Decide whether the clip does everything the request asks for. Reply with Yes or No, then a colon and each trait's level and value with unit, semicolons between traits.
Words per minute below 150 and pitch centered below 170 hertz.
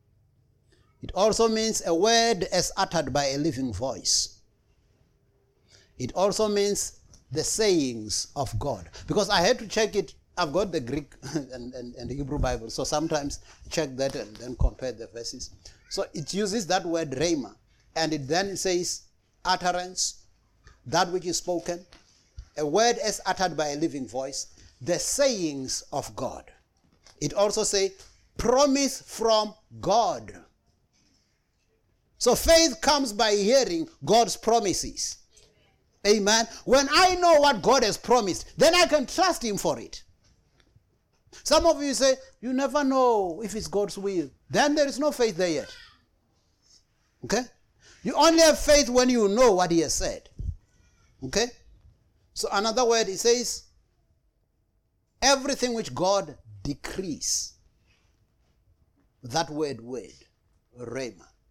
No: average, 140 wpm; medium, 180 Hz